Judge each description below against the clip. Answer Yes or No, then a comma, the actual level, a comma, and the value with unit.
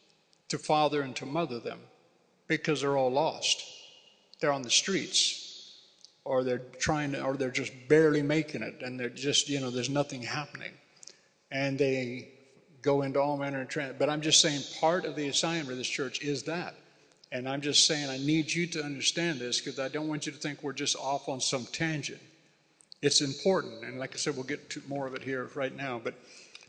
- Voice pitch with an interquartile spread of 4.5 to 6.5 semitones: No, narrow, 2.6 semitones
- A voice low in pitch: No, medium, 145 Hz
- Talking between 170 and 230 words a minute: Yes, fast, 205 wpm